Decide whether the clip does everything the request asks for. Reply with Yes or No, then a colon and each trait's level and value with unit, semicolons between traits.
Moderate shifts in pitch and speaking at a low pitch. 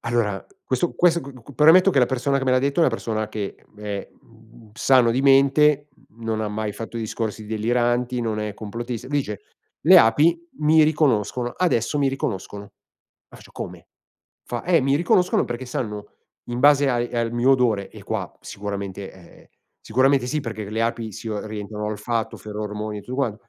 Yes: average, 4.2 semitones; low, 120 Hz